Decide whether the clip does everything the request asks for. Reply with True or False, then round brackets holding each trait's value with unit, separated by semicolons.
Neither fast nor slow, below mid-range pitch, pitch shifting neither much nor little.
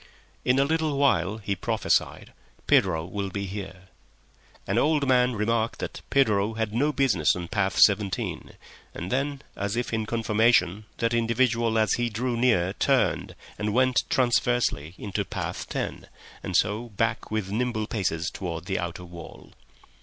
True (155 wpm; 110 Hz; 4.0 semitones)